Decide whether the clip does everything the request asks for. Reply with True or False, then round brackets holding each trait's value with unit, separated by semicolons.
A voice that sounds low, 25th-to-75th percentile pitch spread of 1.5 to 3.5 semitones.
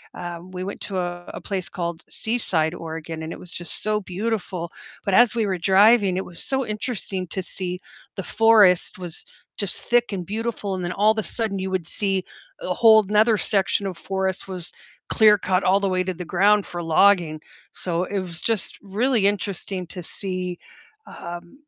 False (190 Hz; 2.9 semitones)